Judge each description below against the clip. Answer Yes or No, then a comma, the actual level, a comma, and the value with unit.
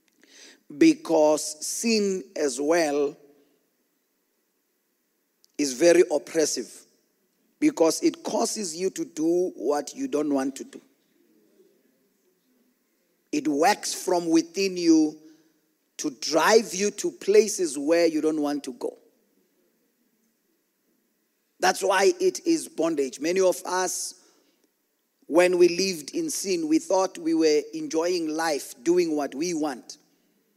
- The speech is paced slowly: Yes, slow, 115 wpm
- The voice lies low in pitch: No, medium, 185 Hz